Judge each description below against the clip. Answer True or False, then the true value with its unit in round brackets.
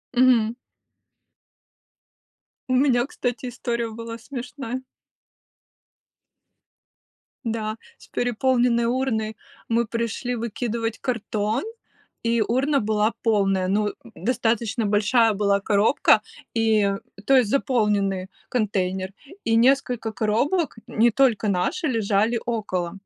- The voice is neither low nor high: False (230 Hz)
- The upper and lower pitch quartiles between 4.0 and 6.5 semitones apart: False (2.7 semitones)